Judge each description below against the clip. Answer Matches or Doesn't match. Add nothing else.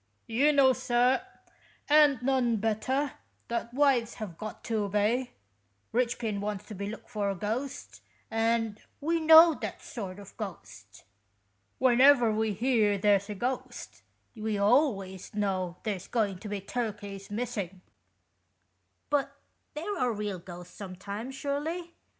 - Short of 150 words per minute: Matches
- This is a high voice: Matches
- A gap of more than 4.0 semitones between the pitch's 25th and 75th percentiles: Matches